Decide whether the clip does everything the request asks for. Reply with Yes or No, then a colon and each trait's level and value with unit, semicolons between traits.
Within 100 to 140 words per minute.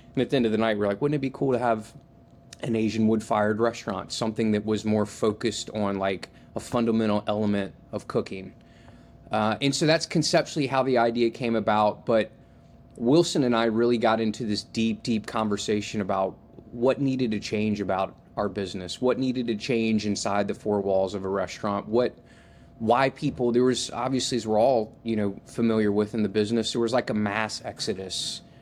No: average, 195 wpm